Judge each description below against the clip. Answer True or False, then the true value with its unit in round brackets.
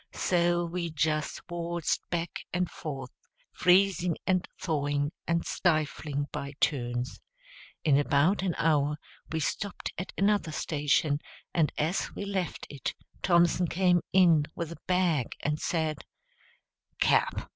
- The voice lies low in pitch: False (165 Hz)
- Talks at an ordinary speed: False (125 wpm)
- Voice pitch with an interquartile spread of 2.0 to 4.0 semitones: True (3.2 semitones)